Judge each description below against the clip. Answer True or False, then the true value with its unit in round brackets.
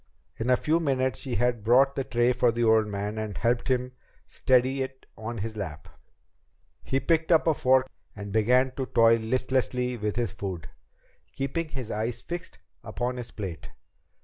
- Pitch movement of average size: True (3.2 semitones)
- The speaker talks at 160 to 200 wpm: True (175 wpm)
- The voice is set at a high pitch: False (120 Hz)